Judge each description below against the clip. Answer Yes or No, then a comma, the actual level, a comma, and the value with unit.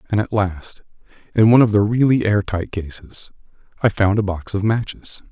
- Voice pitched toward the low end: Yes, low, 105 Hz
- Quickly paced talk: No, average, 190 wpm